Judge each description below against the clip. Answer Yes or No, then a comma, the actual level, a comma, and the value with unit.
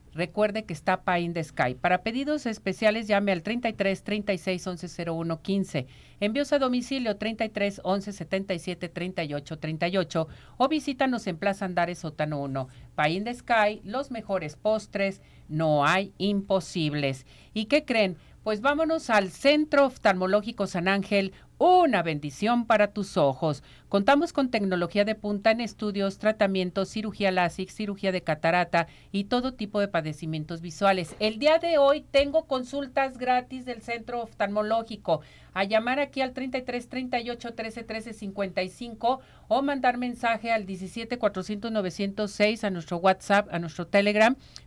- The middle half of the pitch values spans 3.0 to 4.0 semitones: No, average, 4.5 semitones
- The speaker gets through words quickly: No, average, 140 wpm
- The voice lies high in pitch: Yes, high, 205 Hz